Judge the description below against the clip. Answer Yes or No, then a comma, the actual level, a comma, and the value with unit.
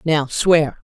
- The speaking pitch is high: No, medium, 150 Hz